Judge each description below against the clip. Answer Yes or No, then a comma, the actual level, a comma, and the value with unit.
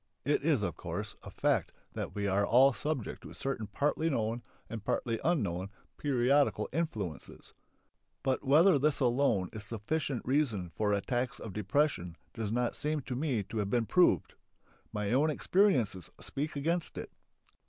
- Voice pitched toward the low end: Yes, low, 120 Hz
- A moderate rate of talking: Yes, average, 155 wpm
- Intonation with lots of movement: Yes, wide, 6.0 semitones